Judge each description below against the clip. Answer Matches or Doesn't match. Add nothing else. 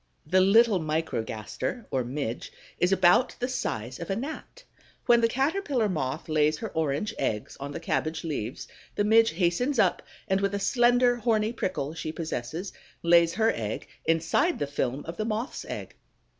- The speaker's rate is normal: Matches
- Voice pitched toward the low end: Doesn't match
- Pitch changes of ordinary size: Doesn't match